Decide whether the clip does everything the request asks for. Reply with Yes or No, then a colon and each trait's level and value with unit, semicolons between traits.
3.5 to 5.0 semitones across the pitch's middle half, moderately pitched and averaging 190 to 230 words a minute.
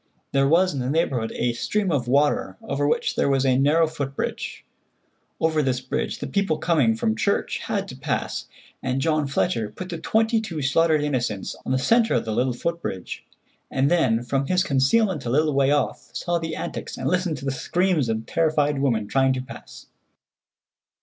Yes: average, 4.3 semitones; medium, 145 Hz; average, 195 wpm